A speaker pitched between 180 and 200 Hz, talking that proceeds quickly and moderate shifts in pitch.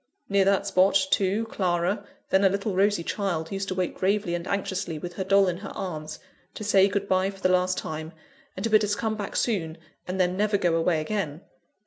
No: high, 190 Hz; fast, 215 wpm; narrow, 2.2 semitones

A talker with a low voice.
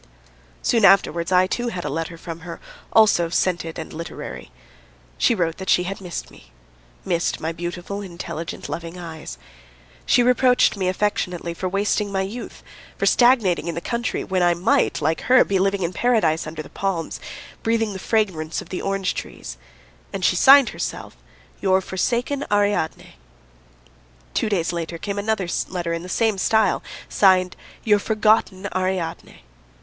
No: medium, 185 Hz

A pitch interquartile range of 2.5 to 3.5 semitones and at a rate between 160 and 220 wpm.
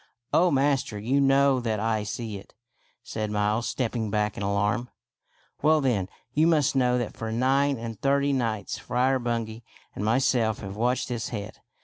No: average, 3.9 semitones; average, 175 wpm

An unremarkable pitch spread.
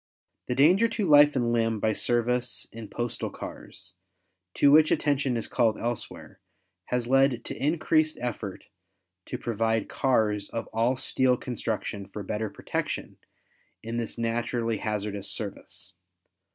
Yes: average, 3.1 semitones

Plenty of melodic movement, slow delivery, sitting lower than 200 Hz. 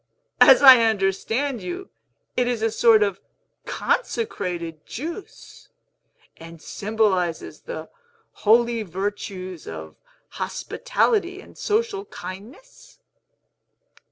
No: wide, 8.0 semitones; slow, 90 wpm; high, 225 Hz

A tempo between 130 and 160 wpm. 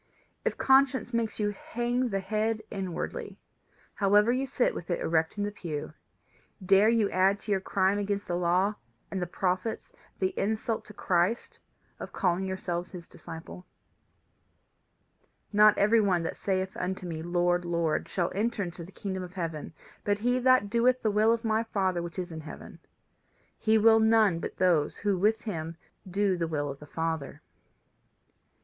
No: average, 170 wpm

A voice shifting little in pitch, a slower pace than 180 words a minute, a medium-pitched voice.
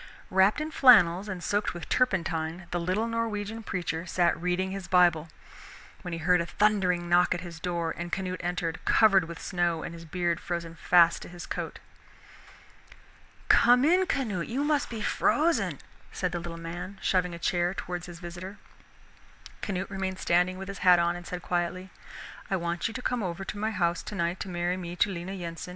No: narrow, 2.3 semitones; average, 190 wpm; medium, 180 Hz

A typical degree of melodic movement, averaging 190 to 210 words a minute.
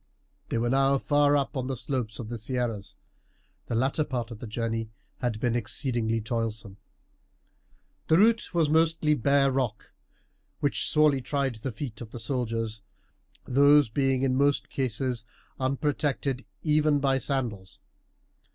No: average, 3.7 semitones; average, 140 wpm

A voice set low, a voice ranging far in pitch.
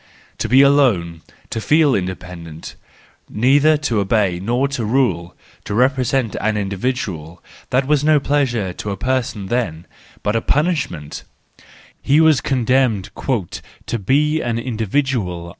Yes: low, 120 Hz; wide, 6.1 semitones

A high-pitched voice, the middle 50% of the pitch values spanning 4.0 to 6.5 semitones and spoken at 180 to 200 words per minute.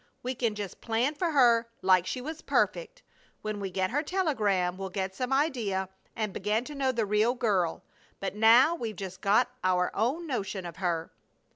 Yes: high, 220 Hz; wide, 5.4 semitones; average, 185 wpm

